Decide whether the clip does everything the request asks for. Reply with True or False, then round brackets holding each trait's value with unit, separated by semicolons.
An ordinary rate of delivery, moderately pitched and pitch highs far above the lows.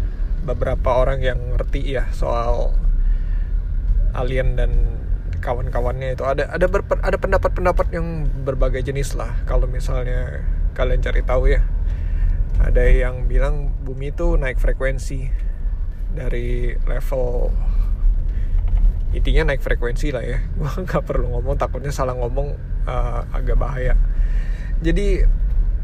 False (115 wpm; 90 Hz; 8.1 semitones)